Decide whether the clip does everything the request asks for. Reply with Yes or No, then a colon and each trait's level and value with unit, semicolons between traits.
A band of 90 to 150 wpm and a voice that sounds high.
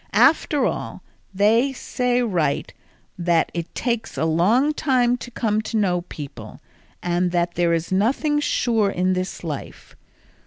Yes: average, 145 wpm; high, 200 Hz